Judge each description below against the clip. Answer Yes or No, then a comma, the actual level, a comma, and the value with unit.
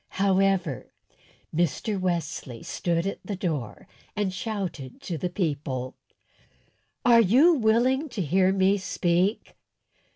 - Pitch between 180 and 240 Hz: Yes, high, 190 Hz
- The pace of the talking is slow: Yes, slow, 110 wpm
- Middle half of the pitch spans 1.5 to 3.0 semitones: No, average, 3.7 semitones